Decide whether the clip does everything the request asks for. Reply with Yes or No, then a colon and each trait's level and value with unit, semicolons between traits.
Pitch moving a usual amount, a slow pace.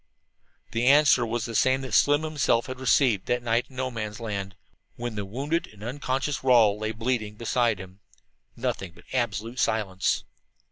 No: average, 3.6 semitones; average, 170 wpm